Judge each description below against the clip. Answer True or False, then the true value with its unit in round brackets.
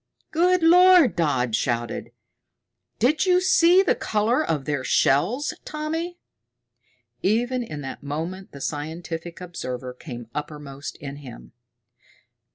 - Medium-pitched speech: True (170 Hz)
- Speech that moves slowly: True (115 wpm)